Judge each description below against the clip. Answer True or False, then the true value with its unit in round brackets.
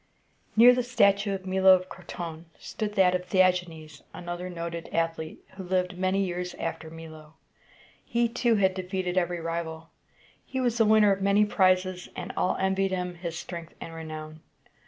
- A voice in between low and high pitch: True (180 Hz)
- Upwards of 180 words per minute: False (175 wpm)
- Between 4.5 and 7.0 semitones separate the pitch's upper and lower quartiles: False (2.6 semitones)